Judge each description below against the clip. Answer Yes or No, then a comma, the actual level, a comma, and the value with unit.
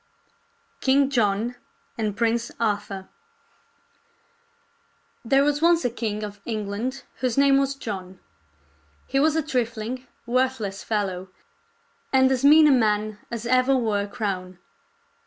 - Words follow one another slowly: Yes, slow, 125 wpm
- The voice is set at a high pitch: Yes, high, 235 Hz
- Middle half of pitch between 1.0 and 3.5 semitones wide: No, average, 4.2 semitones